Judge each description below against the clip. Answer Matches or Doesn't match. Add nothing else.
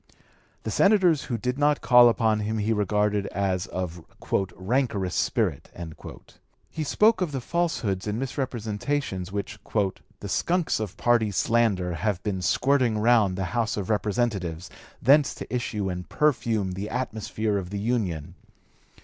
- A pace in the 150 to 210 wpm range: Doesn't match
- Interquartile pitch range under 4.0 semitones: Doesn't match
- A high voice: Doesn't match